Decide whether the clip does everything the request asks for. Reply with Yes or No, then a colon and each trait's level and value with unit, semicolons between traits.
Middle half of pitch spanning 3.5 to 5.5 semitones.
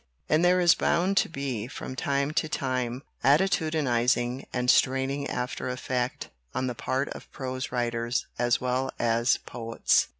No: narrow, 2.4 semitones